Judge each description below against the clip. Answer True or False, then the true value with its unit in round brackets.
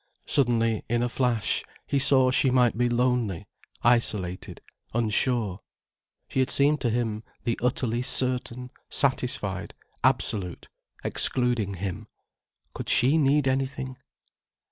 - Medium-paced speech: False (115 wpm)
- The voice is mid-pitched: False (120 Hz)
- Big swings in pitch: False (2.9 semitones)